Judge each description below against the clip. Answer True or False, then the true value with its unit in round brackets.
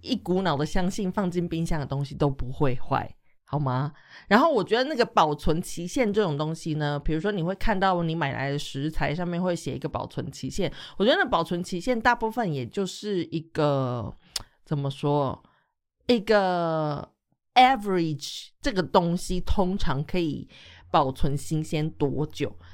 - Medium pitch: True (160 Hz)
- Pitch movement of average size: True (4.4 semitones)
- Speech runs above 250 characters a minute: True (265 characters per minute)